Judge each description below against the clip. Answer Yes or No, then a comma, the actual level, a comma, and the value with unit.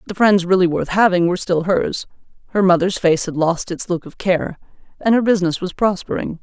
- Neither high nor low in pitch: Yes, medium, 180 Hz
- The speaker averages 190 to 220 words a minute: Yes, fast, 205 wpm